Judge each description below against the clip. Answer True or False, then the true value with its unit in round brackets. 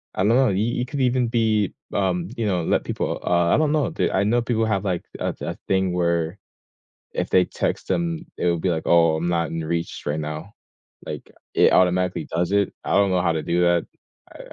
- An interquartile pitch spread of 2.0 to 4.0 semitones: False (4.5 semitones)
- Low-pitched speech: True (90 Hz)